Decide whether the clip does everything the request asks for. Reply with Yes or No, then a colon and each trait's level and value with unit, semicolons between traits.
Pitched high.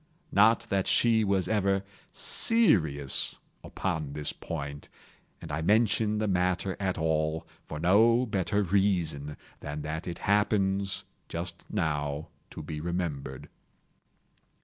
No: very low, 90 Hz